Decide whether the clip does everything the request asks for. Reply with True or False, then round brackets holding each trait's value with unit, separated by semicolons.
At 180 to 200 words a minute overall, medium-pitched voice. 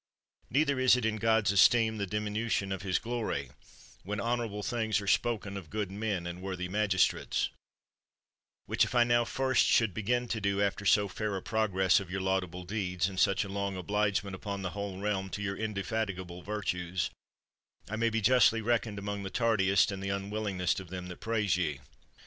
False (190 wpm; 100 Hz)